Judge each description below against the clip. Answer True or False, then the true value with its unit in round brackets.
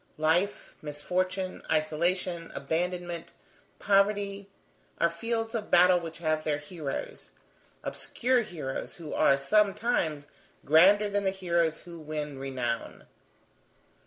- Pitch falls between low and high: True (170 Hz)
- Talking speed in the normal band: False (110 wpm)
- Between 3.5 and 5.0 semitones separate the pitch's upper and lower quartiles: True (4.2 semitones)